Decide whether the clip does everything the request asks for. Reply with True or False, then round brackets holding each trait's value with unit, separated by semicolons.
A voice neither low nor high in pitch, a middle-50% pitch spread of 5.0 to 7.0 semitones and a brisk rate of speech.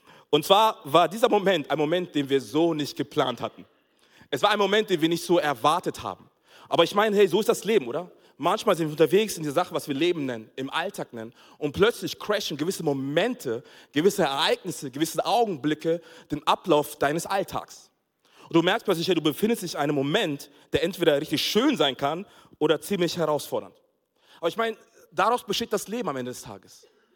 True (165 Hz; 5.3 semitones; 200 wpm)